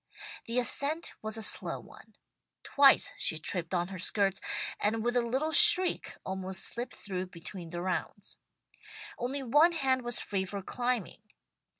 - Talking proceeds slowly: No, average, 155 wpm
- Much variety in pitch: Yes, wide, 5.7 semitones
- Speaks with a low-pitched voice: No, high, 225 Hz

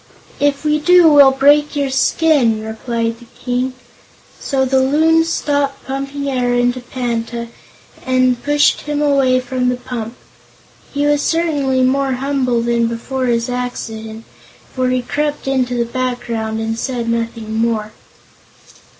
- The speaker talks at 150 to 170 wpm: No, average, 140 wpm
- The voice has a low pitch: No, very high, 255 Hz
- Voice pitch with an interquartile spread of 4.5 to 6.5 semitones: No, average, 3.1 semitones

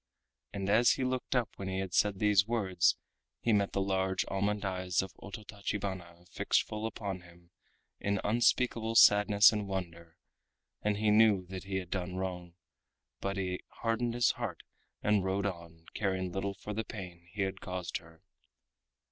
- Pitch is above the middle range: No, very low, 95 Hz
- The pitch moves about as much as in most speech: No, narrow, 2.3 semitones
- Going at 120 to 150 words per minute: No, average, 165 wpm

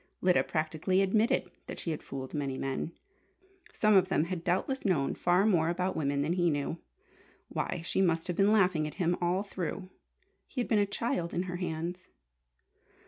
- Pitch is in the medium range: Yes, medium, 175 Hz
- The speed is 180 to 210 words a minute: Yes, average, 185 wpm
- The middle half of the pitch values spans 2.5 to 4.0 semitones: Yes, average, 3.0 semitones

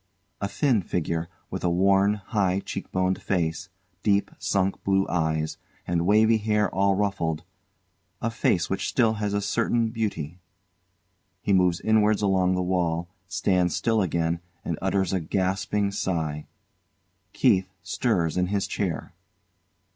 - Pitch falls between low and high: No, very low, 95 Hz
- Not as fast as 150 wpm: Yes, average, 140 wpm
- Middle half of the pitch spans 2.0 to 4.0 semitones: Yes, average, 2.8 semitones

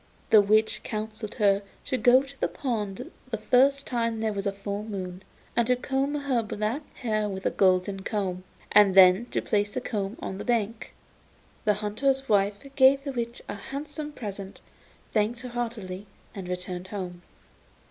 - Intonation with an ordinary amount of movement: Yes, average, 3.8 semitones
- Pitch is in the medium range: No, high, 215 Hz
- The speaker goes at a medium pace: Yes, average, 170 wpm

